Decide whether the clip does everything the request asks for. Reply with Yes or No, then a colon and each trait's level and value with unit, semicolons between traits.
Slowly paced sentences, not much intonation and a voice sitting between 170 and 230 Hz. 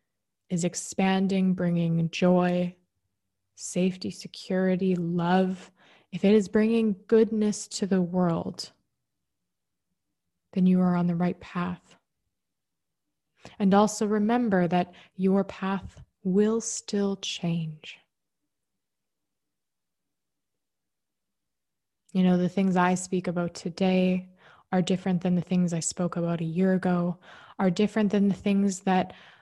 Yes: slow, 115 wpm; narrow, 1.9 semitones; medium, 185 Hz